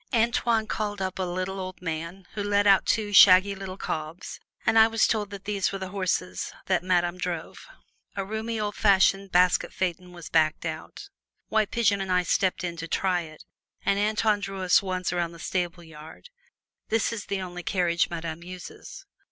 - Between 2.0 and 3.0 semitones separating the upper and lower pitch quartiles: Yes, average, 2.7 semitones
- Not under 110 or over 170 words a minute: No, average, 185 wpm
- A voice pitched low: No, medium, 185 Hz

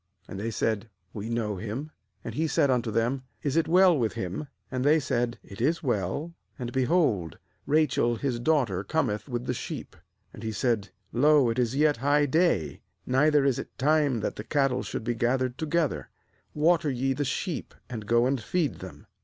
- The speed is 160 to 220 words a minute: Yes, average, 185 wpm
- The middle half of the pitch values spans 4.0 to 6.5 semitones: Yes, average, 4.6 semitones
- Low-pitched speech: Yes, low, 130 Hz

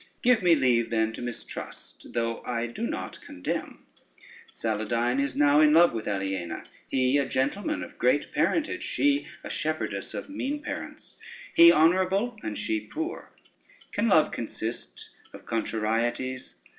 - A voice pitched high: No, low, 130 Hz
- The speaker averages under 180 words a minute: Yes, average, 145 wpm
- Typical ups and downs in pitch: No, wide, 8.2 semitones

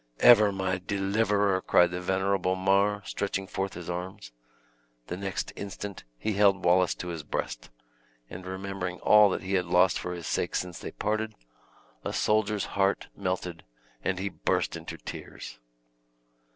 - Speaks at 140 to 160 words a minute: Yes, average, 150 wpm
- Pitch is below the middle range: Yes, very low, 95 Hz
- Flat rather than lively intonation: Yes, narrow, 1.9 semitones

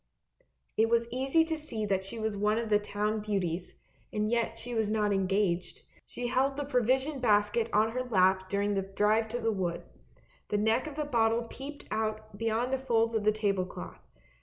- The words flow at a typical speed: Yes, average, 195 wpm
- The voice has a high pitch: Yes, high, 220 Hz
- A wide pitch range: No, average, 2.7 semitones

